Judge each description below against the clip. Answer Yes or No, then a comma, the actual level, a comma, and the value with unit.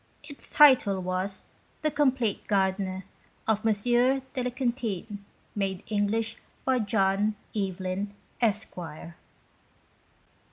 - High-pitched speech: Yes, high, 210 Hz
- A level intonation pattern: No, average, 4.3 semitones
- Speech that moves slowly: Yes, slow, 105 wpm